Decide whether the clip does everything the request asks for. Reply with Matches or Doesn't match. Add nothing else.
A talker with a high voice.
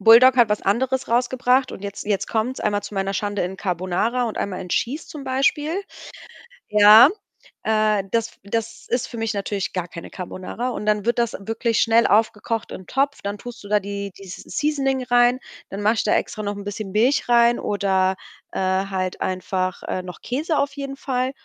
Matches